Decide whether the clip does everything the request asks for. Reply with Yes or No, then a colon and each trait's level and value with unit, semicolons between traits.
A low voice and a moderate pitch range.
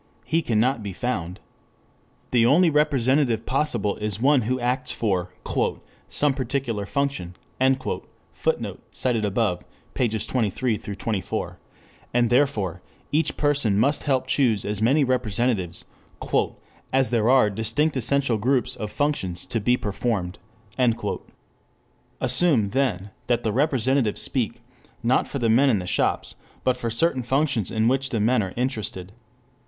Yes: low, 120 Hz; average, 4.0 semitones